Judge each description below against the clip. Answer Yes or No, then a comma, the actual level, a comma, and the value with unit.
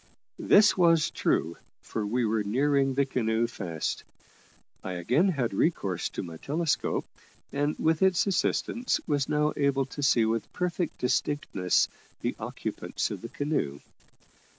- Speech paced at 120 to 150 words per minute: Yes, average, 140 wpm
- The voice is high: No, low, 135 Hz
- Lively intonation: Yes, wide, 5.9 semitones